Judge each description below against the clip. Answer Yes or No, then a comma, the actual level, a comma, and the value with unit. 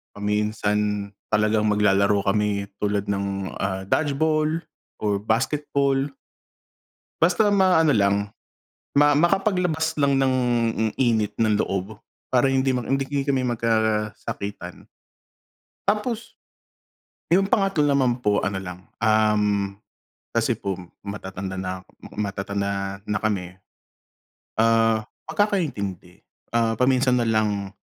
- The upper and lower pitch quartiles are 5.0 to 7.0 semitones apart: Yes, wide, 5.5 semitones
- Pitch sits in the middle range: No, low, 110 Hz